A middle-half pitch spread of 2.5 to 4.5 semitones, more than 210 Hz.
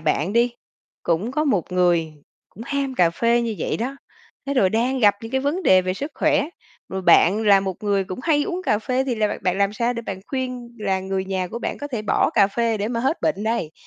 No: average, 4.9 semitones; high, 220 Hz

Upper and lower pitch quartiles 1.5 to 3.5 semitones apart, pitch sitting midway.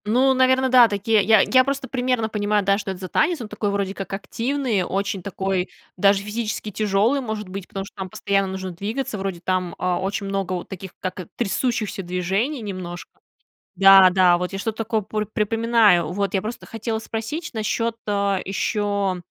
No: average, 2.9 semitones; high, 200 Hz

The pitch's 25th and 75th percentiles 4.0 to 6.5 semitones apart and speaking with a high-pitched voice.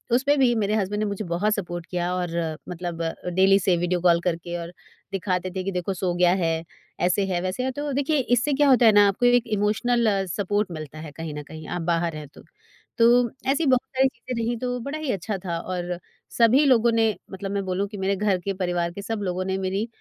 Yes: average, 4.7 semitones; high, 195 Hz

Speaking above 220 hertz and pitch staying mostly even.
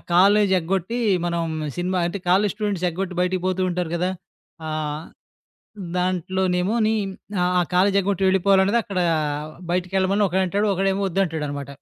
No: medium, 185 Hz; narrow, 1.7 semitones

